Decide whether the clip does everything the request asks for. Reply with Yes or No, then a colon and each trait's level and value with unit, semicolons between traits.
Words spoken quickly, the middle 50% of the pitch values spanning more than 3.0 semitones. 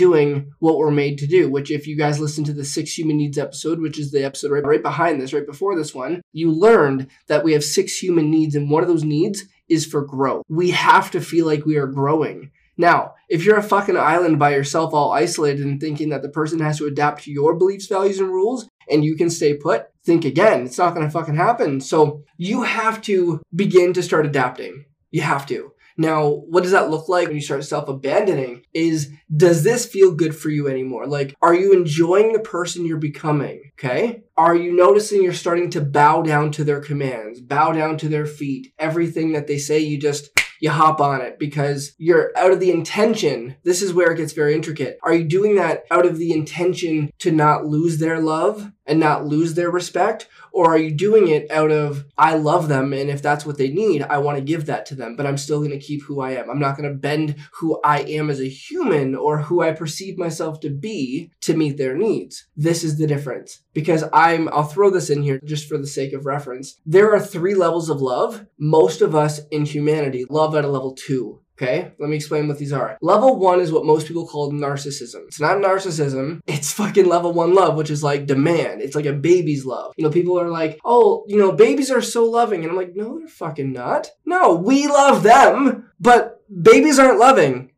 Yes: fast, 225 wpm; average, 3.4 semitones